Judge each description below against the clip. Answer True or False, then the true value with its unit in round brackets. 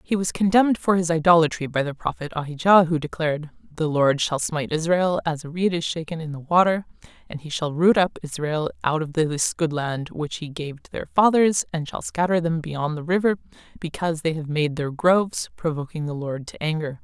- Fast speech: True (210 wpm)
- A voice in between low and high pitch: True (160 Hz)